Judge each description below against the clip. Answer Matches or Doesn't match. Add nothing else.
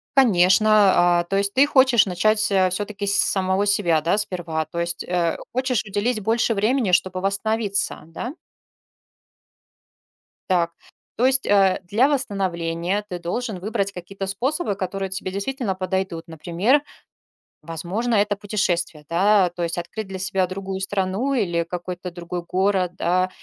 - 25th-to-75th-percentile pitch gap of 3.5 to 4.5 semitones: Doesn't match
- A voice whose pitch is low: Doesn't match